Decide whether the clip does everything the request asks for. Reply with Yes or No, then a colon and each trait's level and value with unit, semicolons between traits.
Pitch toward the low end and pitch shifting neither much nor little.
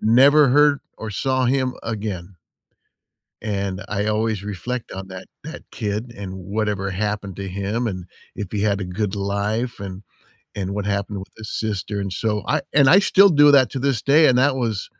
Yes: low, 105 Hz; average, 4.2 semitones